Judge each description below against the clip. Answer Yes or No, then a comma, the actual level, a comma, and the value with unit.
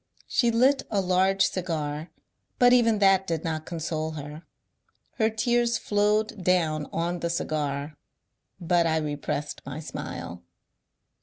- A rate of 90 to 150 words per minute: Yes, slow, 135 wpm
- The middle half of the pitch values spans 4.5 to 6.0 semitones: Yes, average, 5.2 semitones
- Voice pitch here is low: No, medium, 170 Hz